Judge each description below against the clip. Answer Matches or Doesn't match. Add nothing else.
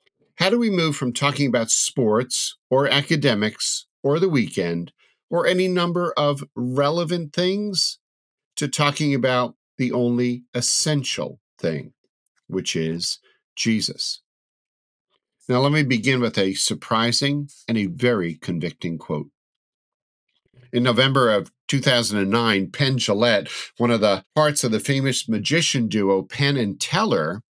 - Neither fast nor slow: Doesn't match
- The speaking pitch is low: Matches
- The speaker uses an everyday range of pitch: Matches